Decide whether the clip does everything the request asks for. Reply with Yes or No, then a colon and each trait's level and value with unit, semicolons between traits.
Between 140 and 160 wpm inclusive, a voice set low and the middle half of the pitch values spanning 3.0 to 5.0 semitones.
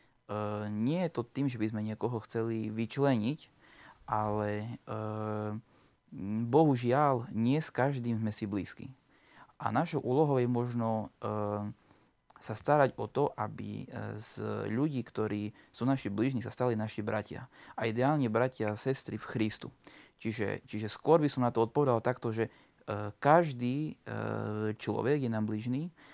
Yes: average, 150 wpm; low, 115 Hz; average, 3.5 semitones